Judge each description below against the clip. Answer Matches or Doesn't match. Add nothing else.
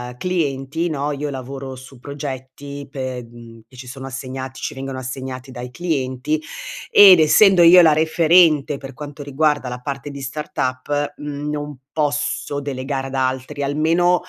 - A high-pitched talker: Doesn't match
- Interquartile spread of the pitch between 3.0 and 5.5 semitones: Doesn't match